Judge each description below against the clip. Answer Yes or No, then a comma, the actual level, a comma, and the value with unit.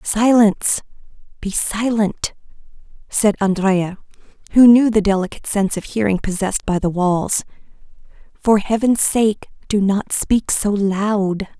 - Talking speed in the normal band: No, slow, 120 wpm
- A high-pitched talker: Yes, high, 205 Hz